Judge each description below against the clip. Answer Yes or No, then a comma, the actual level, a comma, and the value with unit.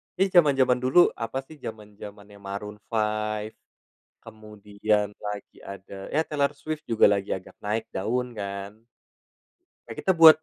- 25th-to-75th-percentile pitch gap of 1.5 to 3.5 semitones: No, average, 3.9 semitones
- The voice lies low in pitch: Yes, low, 105 Hz